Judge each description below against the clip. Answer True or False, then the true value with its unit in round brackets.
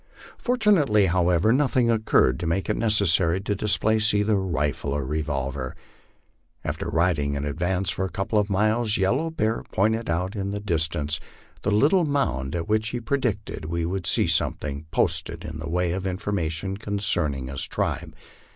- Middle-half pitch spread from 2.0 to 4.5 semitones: False (5.0 semitones)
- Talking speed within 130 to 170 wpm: True (165 wpm)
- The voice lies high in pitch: False (95 Hz)